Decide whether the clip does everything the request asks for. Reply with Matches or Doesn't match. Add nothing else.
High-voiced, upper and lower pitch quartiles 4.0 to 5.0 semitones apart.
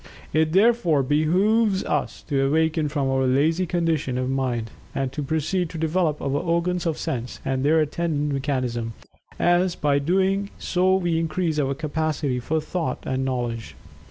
Doesn't match